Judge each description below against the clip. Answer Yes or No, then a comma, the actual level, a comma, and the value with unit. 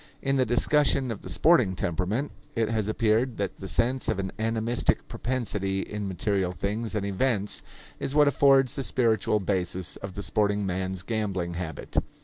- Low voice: Yes, low, 105 Hz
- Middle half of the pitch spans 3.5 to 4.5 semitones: Yes, average, 4.0 semitones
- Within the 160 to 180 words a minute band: Yes, average, 165 wpm